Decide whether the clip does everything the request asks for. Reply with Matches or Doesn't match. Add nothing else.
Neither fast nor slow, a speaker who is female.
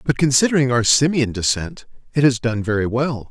Doesn't match